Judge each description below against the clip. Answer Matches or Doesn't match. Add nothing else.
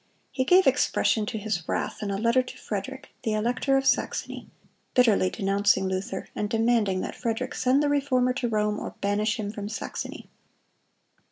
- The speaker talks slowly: Doesn't match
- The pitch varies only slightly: Doesn't match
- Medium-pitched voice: Doesn't match